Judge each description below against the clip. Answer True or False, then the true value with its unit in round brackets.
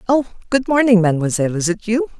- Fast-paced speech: False (190 wpm)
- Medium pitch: False (215 Hz)